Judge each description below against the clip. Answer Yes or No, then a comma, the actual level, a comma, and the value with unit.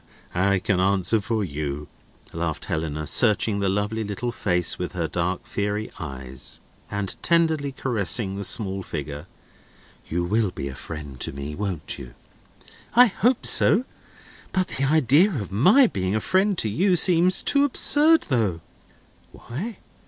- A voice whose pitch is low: Yes, low, 105 Hz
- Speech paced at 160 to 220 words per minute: No, average, 150 wpm